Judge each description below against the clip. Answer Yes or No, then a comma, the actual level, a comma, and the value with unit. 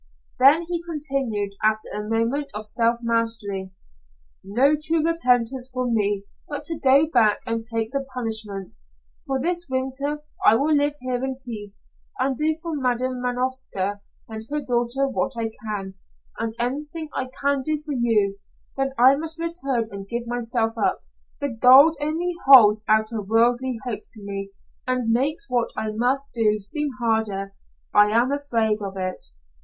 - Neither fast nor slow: Yes, average, 160 wpm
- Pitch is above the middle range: Yes, high, 245 Hz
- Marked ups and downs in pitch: No, average, 4.1 semitones